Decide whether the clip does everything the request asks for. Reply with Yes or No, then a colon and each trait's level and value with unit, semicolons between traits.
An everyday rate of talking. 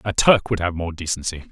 No: fast, 240 wpm